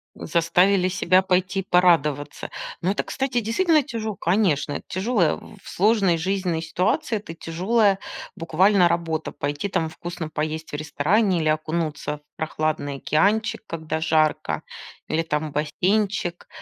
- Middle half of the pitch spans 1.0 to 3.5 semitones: No, average, 4.1 semitones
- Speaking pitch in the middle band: Yes, medium, 175 Hz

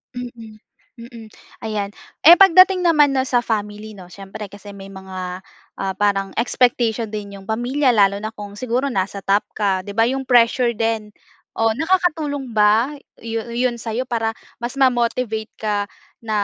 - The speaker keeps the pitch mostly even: No, average, 3.3 semitones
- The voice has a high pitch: Yes, high, 225 Hz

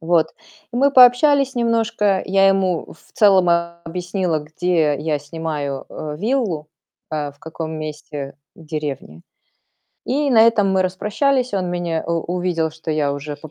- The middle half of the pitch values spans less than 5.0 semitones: No, wide, 5.4 semitones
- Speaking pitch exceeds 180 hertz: No, medium, 175 Hz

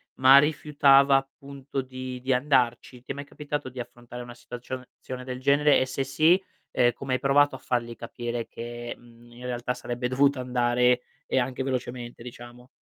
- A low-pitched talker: Yes, low, 125 Hz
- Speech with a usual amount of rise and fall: No, narrow, 2.1 semitones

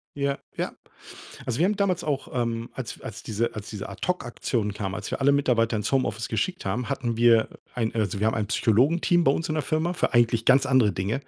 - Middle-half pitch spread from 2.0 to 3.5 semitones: No, average, 4.1 semitones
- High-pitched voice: No, low, 120 Hz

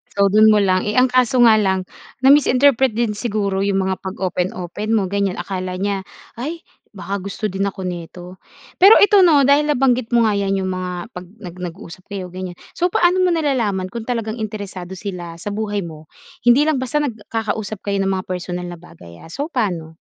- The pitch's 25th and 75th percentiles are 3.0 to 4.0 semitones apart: No, average, 4.6 semitones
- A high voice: Yes, high, 200 Hz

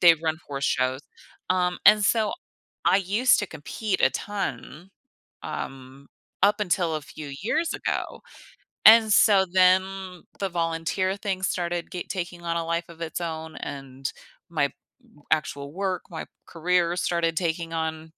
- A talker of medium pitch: Yes, medium, 170 Hz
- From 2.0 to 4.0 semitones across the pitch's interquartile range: Yes, average, 3.1 semitones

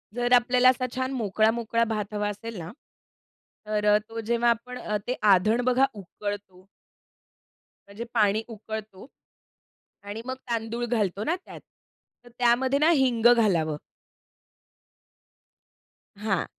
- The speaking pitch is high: Yes, high, 225 Hz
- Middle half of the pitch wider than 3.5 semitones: No, average, 2.9 semitones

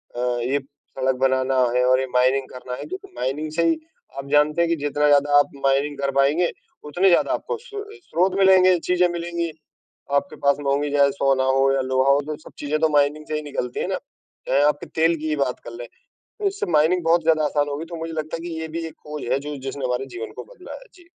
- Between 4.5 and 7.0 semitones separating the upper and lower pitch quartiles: No, average, 3.6 semitones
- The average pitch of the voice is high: No, medium, 150 Hz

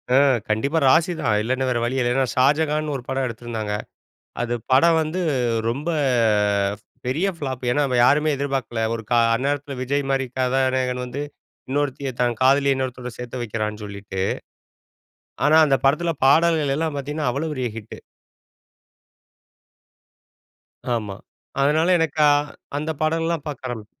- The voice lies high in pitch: No, low, 135 Hz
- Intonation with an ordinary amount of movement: Yes, average, 3.3 semitones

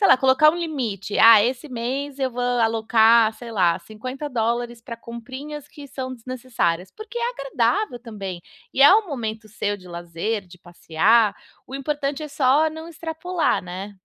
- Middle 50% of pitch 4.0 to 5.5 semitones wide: Yes, average, 4.7 semitones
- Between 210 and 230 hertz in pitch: No, high, 240 Hz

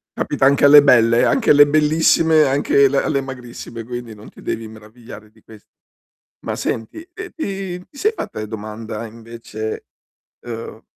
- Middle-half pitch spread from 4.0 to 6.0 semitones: Yes, average, 4.9 semitones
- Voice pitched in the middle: No, low, 120 Hz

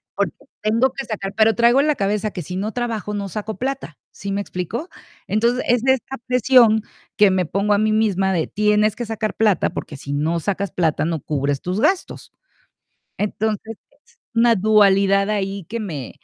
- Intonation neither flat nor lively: Yes, average, 3.0 semitones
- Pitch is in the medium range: No, high, 210 Hz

